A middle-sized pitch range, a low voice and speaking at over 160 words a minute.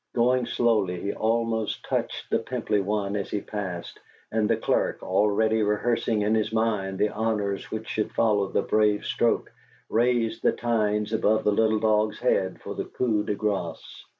No: narrow, 1.5 semitones; low, 105 Hz; average, 170 wpm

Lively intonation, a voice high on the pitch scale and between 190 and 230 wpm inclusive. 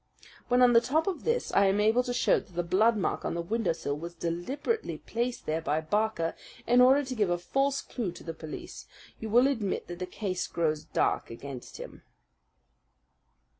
Yes: wide, 6.6 semitones; high, 205 Hz; average, 195 wpm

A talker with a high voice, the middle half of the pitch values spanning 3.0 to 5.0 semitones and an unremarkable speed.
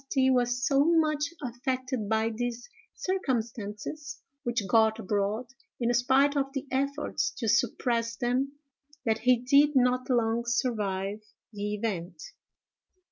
No: high, 245 Hz; average, 3.5 semitones; slow, 125 wpm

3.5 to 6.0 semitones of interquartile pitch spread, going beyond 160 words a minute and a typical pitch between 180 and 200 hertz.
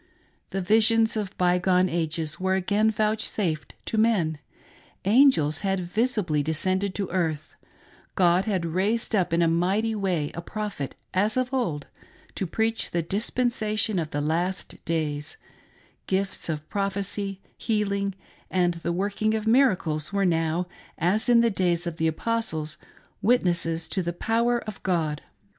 No: average, 4.3 semitones; average, 145 wpm; high, 190 Hz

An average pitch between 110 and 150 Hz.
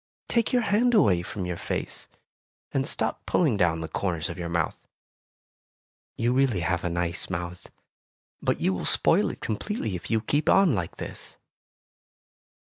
No: very low, 95 Hz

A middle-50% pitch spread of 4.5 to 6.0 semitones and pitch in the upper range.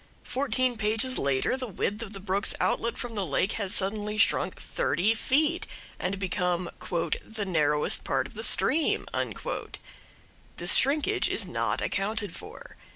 Yes: average, 5.0 semitones; high, 210 Hz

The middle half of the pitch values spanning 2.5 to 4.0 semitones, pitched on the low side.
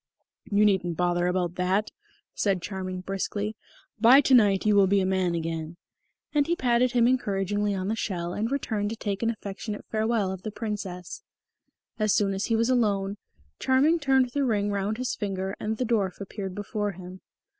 No: average, 3.2 semitones; high, 205 Hz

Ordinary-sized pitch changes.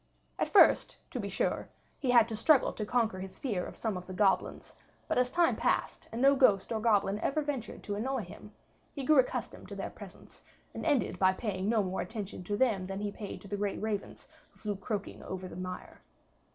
Yes: average, 4.1 semitones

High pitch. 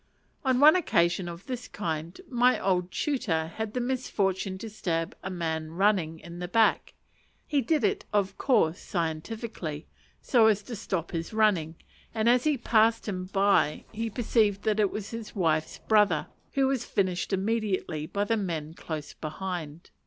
Yes: high, 195 Hz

